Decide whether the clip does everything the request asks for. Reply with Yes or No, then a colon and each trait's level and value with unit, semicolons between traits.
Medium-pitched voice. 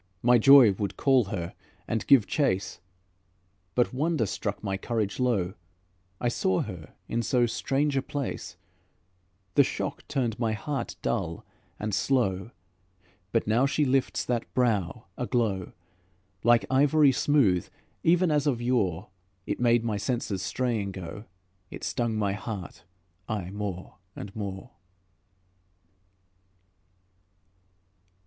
No: low, 115 Hz